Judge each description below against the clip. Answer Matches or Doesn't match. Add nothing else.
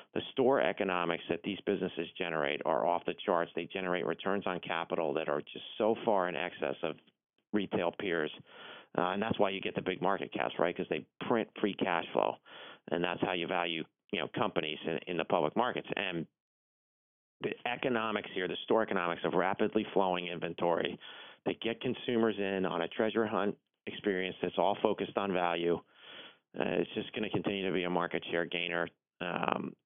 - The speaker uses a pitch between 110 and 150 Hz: Doesn't match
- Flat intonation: Doesn't match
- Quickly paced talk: Doesn't match